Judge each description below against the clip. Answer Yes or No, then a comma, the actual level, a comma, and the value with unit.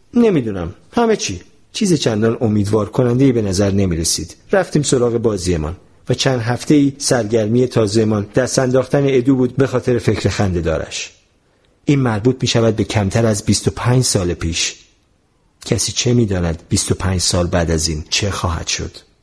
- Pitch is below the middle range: Yes, low, 115 Hz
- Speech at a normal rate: No, fast, 160 wpm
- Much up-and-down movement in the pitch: No, average, 4.5 semitones